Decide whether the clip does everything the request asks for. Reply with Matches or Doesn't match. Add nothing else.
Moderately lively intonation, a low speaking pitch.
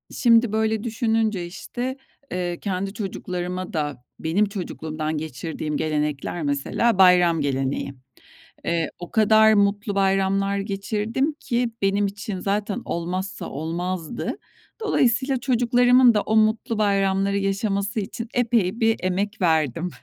Doesn't match